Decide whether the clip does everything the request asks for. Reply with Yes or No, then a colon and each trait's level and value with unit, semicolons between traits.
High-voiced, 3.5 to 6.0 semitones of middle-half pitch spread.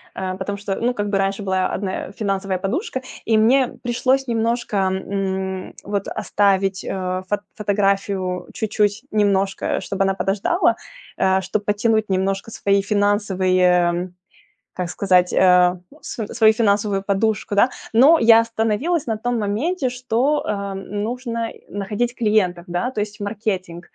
No: high, 205 Hz; average, 2.9 semitones